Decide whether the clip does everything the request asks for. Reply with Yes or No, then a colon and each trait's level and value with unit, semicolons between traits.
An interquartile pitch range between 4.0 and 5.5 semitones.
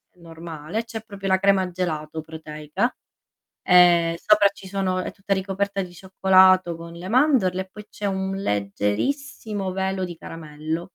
No: average, 2.9 semitones